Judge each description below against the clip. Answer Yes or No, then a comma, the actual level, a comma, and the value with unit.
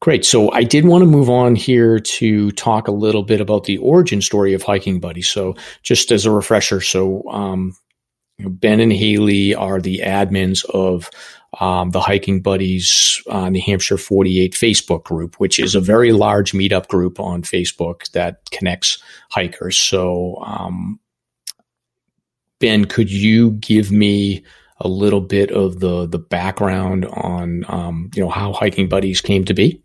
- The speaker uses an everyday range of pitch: No, narrow, 2.1 semitones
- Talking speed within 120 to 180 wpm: Yes, average, 165 wpm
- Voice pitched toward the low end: Yes, low, 100 Hz